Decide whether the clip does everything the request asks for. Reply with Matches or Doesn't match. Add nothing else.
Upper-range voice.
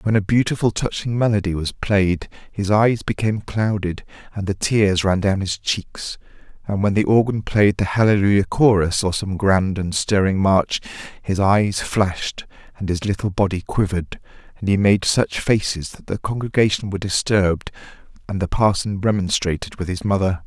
Doesn't match